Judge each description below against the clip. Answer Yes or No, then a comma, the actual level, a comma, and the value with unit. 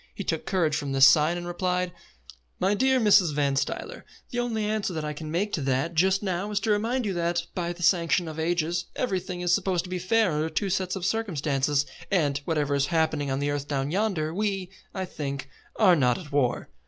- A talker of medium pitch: Yes, medium, 175 Hz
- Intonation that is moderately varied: Yes, average, 4.3 semitones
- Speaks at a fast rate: Yes, fast, 215 wpm